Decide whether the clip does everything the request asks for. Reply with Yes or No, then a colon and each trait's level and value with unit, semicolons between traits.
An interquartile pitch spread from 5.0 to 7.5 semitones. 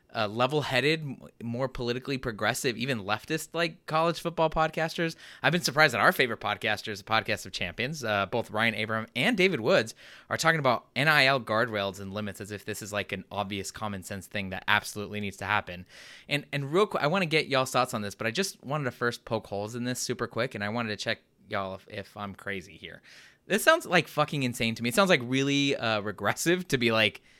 Yes: wide, 5.4 semitones